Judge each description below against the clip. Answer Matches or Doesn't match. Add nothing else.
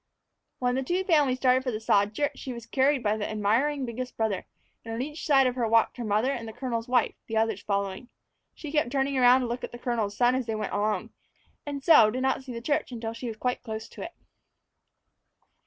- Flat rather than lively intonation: Doesn't match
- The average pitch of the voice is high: Matches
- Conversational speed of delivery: Doesn't match